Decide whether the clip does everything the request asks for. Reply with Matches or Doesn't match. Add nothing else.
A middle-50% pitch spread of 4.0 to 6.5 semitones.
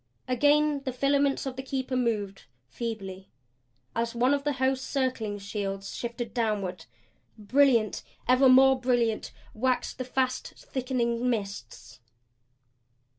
Doesn't match